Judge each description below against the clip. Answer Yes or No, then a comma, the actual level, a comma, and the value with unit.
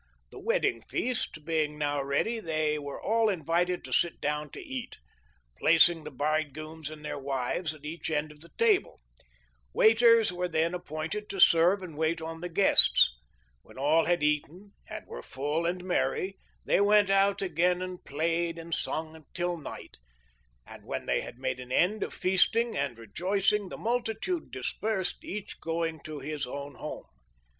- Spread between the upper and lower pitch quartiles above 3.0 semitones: Yes, average, 4.3 semitones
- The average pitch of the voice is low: No, medium, 165 Hz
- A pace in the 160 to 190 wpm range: Yes, average, 165 wpm